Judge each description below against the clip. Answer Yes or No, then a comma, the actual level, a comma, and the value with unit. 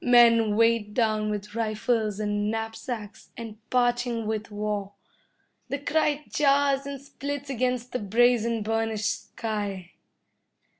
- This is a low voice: No, high, 225 Hz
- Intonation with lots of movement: No, average, 2.9 semitones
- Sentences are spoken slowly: Yes, slow, 115 wpm